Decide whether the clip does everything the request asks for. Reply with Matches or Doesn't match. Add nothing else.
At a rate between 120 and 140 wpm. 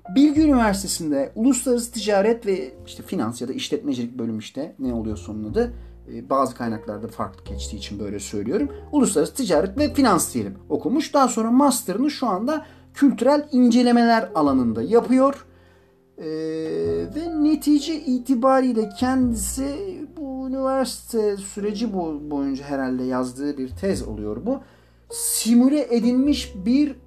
Matches